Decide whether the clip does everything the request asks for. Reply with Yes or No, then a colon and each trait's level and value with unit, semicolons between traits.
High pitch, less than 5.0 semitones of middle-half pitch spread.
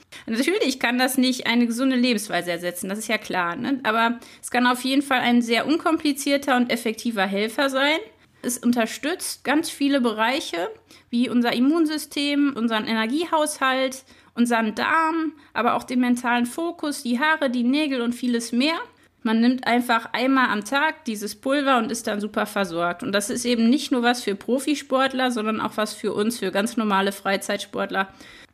Yes: high, 245 Hz; average, 3.7 semitones